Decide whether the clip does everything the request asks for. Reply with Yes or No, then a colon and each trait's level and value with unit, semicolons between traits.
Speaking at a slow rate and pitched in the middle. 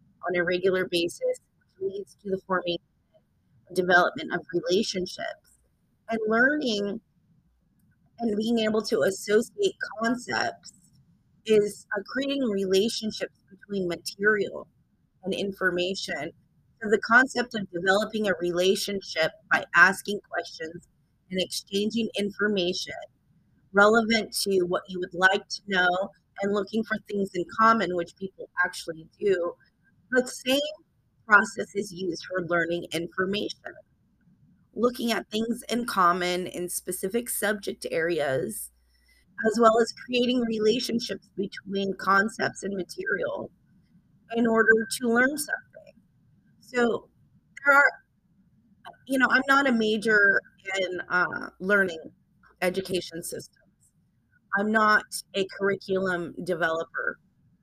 No: slow, 115 wpm; high, 200 Hz